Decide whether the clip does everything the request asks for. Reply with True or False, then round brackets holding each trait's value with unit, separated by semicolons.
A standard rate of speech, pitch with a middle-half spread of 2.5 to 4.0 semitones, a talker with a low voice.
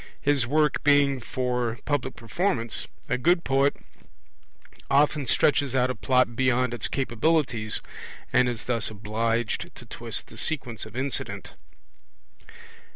False (125 wpm; 3.3 semitones; 130 Hz)